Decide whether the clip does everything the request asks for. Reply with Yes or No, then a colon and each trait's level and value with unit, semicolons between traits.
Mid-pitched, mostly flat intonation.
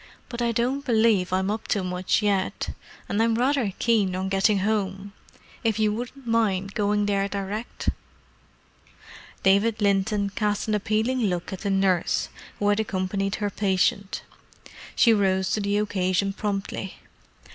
No: high, 205 Hz; narrow, 2.3 semitones